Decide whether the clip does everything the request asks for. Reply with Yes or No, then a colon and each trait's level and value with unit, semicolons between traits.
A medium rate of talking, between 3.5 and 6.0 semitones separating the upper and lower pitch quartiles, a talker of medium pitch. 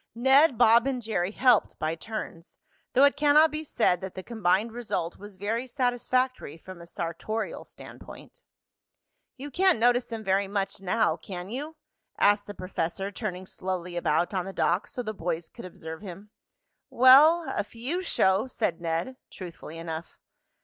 No: average, 160 wpm; wide, 5.6 semitones; high, 205 Hz